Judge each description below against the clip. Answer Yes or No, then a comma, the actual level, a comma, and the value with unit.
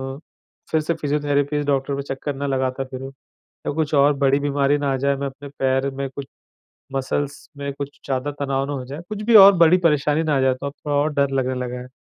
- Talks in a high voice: No, medium, 140 Hz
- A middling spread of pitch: No, narrow, 1.4 semitones